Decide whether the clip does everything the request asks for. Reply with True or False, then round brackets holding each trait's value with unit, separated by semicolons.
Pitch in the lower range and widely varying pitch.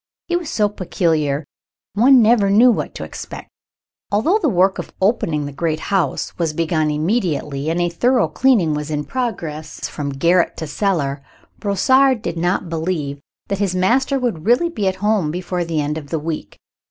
False (180 Hz; 6.0 semitones)